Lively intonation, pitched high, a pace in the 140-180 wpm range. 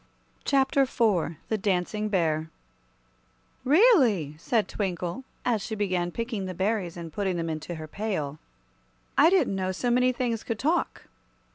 Yes: wide, 5.7 semitones; high, 205 Hz; average, 145 wpm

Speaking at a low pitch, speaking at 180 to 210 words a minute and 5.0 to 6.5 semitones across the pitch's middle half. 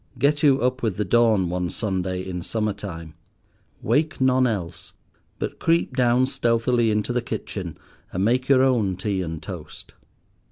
No: low, 110 Hz; average, 160 wpm; wide, 5.6 semitones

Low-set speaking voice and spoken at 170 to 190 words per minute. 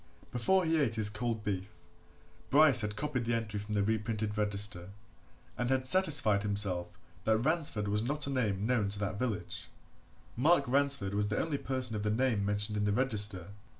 Yes: low, 110 Hz; average, 185 wpm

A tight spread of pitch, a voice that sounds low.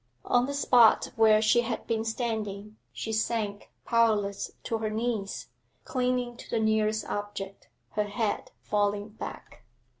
No: narrow, 2.0 semitones; high, 220 Hz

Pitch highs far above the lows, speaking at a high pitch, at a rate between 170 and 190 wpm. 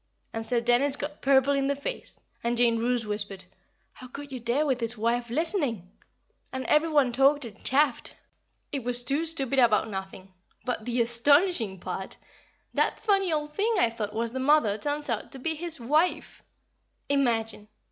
No: average, 4.2 semitones; very high, 255 Hz; average, 175 wpm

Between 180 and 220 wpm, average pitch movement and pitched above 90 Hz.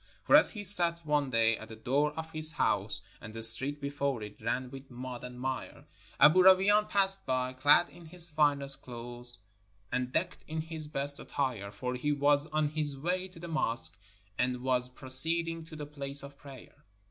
Yes: average, 190 wpm; average, 3.9 semitones; medium, 140 Hz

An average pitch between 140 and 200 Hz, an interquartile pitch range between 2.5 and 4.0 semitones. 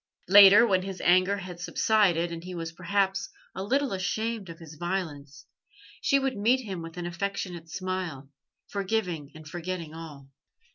Yes: medium, 185 Hz; average, 3.2 semitones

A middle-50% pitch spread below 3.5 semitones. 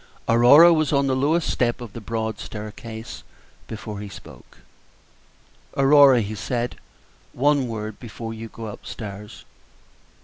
No: average, 3.8 semitones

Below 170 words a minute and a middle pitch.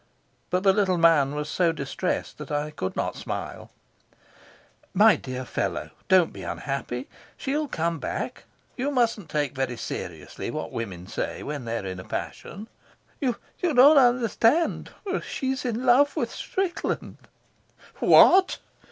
Yes: slow, 135 wpm; medium, 180 Hz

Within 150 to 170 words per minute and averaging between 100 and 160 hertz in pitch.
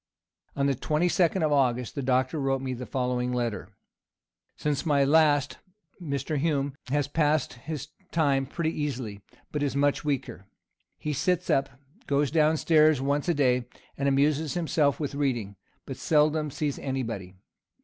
Yes: average, 160 wpm; medium, 140 Hz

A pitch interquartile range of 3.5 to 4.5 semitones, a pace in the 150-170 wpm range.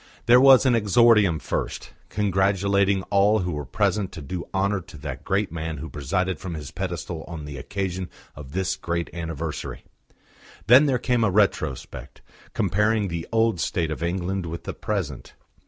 Yes: average, 4.0 semitones; average, 165 wpm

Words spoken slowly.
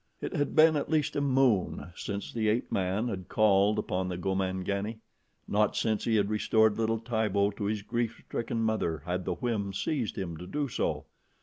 No: average, 190 wpm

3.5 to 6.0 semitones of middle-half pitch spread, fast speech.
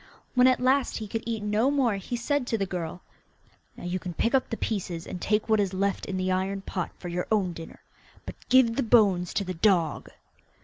Yes: average, 4.2 semitones; fast, 225 wpm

